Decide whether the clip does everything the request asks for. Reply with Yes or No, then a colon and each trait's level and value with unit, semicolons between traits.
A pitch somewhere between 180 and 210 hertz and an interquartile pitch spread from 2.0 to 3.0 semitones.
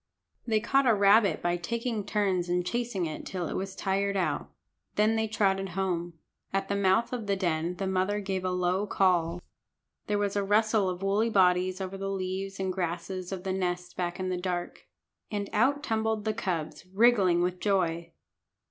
Yes: high, 190 Hz; narrow, 2.4 semitones